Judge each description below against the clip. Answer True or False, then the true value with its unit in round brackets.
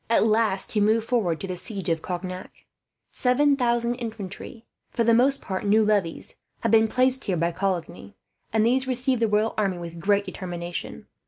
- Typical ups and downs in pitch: True (4.3 semitones)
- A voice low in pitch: False (215 Hz)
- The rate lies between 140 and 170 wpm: False (180 wpm)